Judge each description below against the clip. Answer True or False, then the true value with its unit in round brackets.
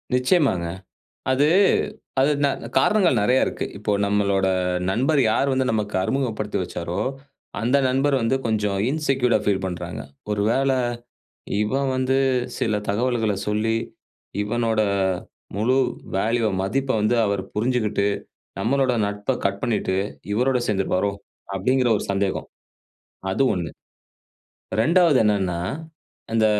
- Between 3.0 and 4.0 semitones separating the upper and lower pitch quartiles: False (4.5 semitones)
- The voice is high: False (110 Hz)